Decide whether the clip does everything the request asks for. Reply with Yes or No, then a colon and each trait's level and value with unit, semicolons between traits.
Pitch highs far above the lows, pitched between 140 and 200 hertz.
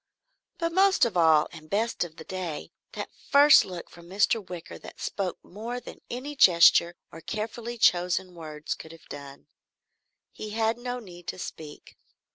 Yes: wide, 5.8 semitones; medium, 185 Hz